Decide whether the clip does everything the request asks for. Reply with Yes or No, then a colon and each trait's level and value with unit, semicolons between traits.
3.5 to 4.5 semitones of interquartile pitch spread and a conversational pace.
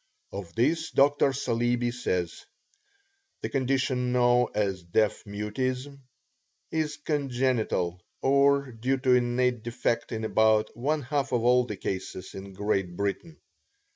No: average, 4.1 semitones; slow, 125 wpm